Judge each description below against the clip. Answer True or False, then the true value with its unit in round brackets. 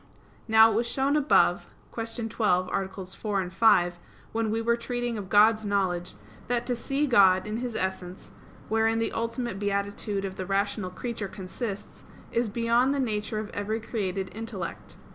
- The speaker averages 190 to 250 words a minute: False (160 wpm)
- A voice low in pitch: False (215 Hz)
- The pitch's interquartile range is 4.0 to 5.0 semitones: False (3.2 semitones)